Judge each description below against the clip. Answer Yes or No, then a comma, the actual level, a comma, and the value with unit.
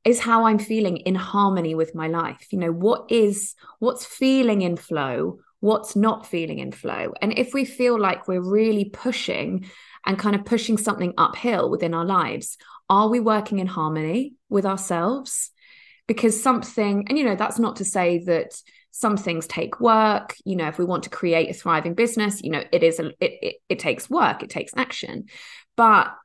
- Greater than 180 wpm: Yes, average, 190 wpm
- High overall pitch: Yes, high, 215 Hz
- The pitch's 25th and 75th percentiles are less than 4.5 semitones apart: No, average, 4.9 semitones